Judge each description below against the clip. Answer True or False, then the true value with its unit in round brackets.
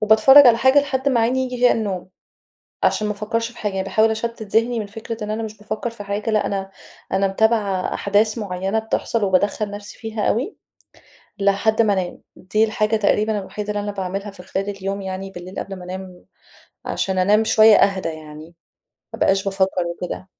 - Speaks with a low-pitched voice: False (210 Hz)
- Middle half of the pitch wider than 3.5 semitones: False (2.4 semitones)